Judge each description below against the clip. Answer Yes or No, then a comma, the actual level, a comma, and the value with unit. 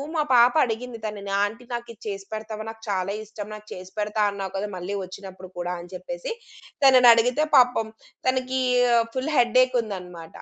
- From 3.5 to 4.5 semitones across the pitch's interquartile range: Yes, average, 4.1 semitones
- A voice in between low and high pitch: No, high, 215 Hz